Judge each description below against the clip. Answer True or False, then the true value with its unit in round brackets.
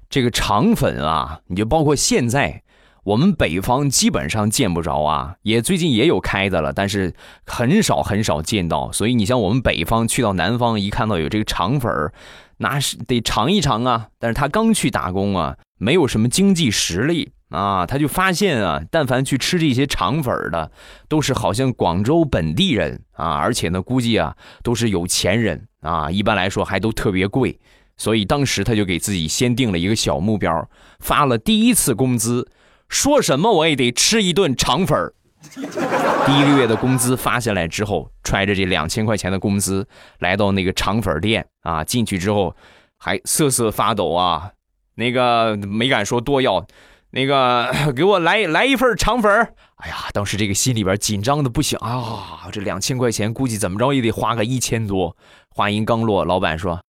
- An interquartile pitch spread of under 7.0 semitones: True (5.2 semitones)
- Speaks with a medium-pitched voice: False (115 Hz)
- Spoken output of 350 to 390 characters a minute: False (275 characters per minute)